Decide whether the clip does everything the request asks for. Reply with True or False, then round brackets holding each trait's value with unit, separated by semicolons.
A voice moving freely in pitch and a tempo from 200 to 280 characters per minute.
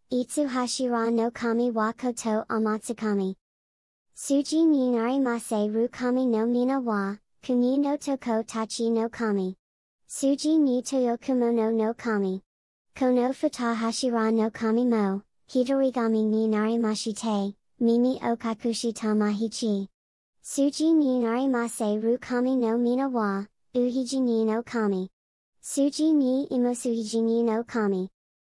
False (2.5 semitones; 270 characters per minute)